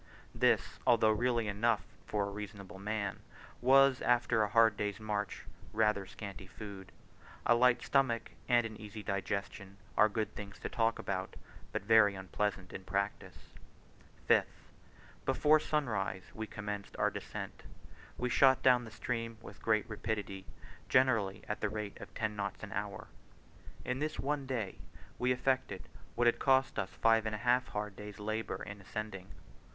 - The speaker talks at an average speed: Yes, average, 155 wpm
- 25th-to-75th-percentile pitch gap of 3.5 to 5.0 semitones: No, average, 3.0 semitones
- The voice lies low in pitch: Yes, low, 110 Hz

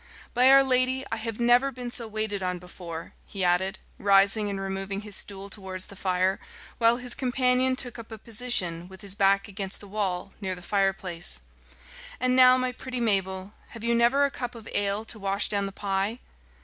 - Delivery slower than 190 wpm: No, average, 195 wpm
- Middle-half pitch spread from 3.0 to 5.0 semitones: Yes, average, 3.9 semitones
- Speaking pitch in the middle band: No, high, 205 Hz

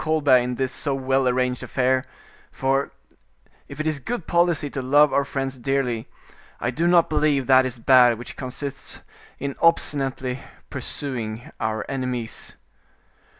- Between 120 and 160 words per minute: Yes, average, 145 wpm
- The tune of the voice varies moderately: No, narrow, 2.2 semitones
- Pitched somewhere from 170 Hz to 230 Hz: No, low, 135 Hz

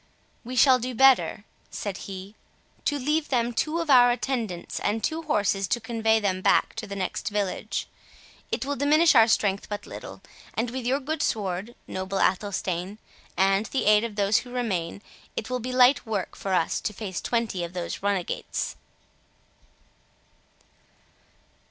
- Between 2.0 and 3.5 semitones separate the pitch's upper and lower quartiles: No, average, 4.4 semitones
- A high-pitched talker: Yes, high, 220 Hz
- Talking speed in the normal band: Yes, average, 160 wpm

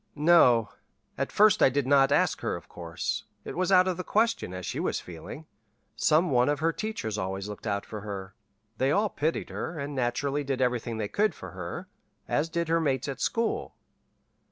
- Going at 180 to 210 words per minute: Yes, average, 200 wpm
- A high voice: No, medium, 140 Hz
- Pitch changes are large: Yes, wide, 7.5 semitones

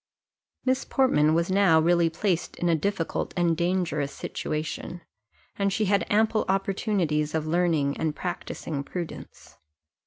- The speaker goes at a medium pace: No, slow, 130 wpm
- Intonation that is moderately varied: Yes, average, 3.7 semitones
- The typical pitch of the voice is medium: Yes, medium, 175 Hz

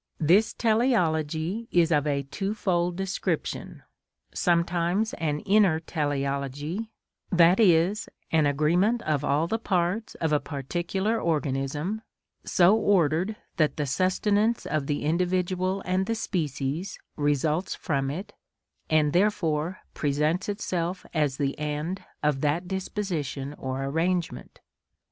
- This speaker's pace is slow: Yes, slow, 115 wpm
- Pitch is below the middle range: No, medium, 170 Hz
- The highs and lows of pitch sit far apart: No, average, 4.3 semitones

